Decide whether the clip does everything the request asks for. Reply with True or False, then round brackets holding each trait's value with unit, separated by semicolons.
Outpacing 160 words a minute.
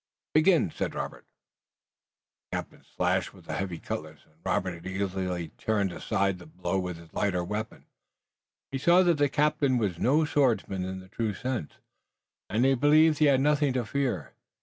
True (170 wpm)